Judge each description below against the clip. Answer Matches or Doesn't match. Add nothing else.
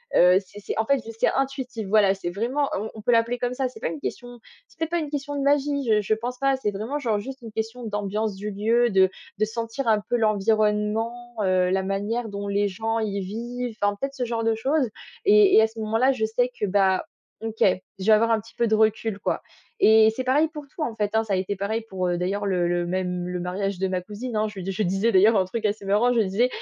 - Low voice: Doesn't match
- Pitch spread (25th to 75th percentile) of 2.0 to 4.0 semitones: Matches